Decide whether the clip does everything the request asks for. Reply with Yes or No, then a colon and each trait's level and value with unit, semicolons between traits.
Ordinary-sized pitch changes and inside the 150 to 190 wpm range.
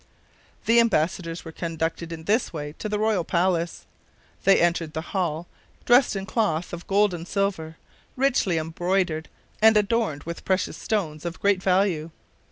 Yes: average, 3.8 semitones; average, 155 wpm